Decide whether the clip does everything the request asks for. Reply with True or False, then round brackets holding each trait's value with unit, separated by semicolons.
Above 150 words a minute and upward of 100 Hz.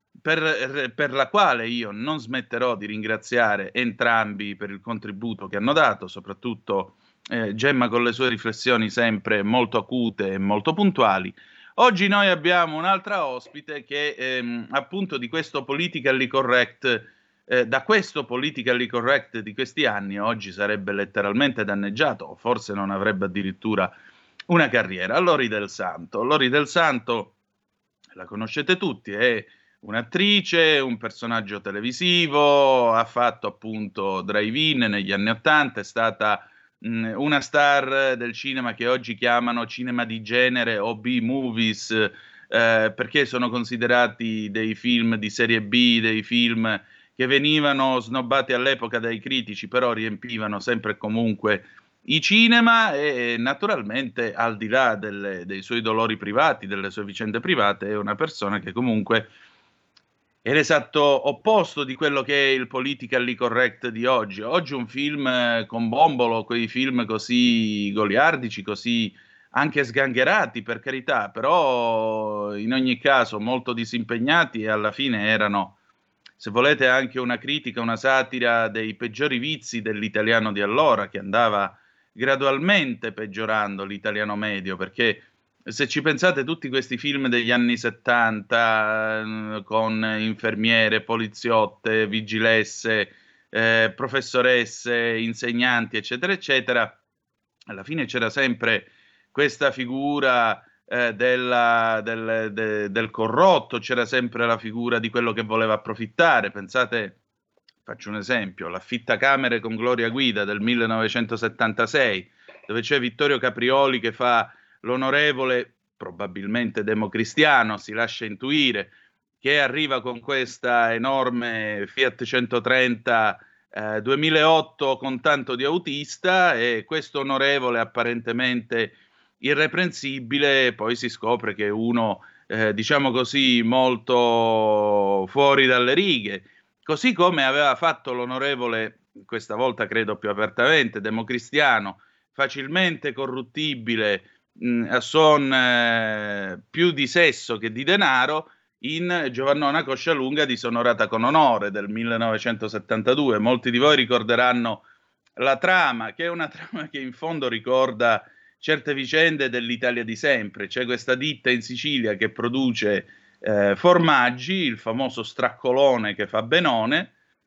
False (125 wpm; 120 Hz)